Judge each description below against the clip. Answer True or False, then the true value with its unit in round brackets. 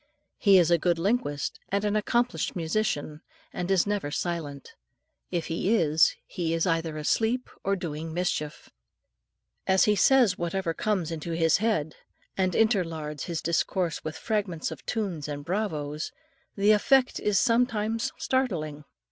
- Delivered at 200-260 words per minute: False (150 wpm)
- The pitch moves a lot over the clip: False (4.8 semitones)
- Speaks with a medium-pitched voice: True (175 Hz)